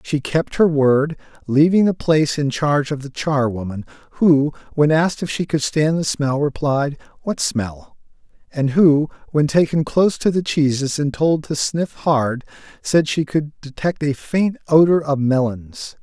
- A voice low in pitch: No, medium, 145 Hz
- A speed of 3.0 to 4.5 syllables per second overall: Yes, 4.4 syllables/s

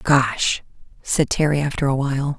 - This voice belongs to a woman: Yes, female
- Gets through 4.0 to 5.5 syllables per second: Yes, 4.6 syllables/s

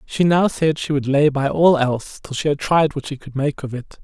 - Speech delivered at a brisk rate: Yes, fast, 285 wpm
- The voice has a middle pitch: Yes, medium, 145 Hz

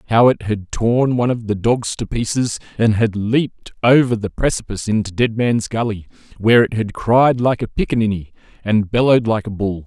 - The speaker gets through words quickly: No, average, 195 wpm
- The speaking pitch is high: No, low, 110 Hz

